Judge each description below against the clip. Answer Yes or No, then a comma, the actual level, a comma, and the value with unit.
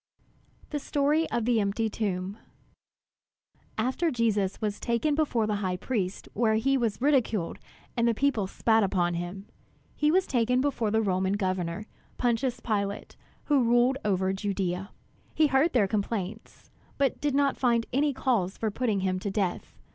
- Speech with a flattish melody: No, average, 4.8 semitones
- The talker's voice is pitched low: No, high, 220 Hz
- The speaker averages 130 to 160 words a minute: Yes, average, 155 wpm